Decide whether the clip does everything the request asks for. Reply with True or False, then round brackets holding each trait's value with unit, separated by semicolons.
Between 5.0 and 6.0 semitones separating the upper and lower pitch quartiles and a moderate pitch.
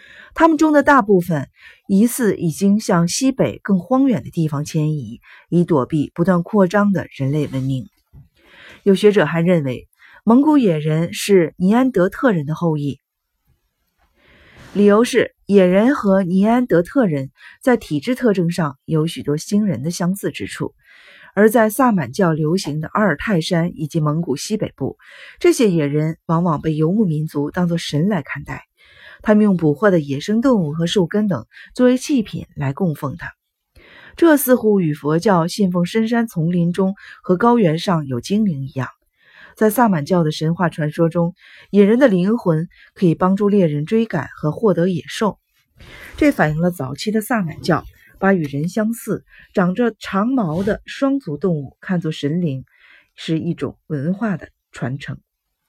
True (5.3 semitones; 180 Hz)